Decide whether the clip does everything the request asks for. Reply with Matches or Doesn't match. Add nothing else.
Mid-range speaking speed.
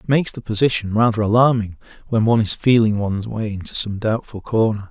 Matches